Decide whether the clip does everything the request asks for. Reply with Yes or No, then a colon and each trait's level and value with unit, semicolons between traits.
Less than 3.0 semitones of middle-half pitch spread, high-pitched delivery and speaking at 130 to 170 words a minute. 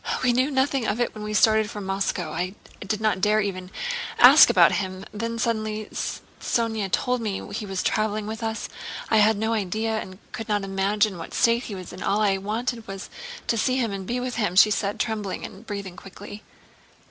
No: narrow, 2.4 semitones; high, 215 Hz; fast, 205 wpm